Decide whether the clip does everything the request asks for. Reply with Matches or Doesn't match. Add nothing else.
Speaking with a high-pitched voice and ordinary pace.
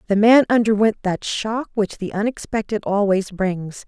Matches